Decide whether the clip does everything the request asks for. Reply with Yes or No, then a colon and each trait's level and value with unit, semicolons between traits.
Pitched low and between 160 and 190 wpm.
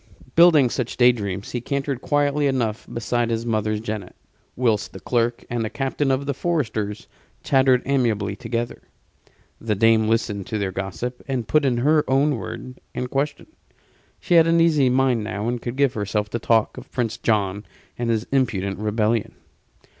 Yes: low, 120 Hz; average, 170 wpm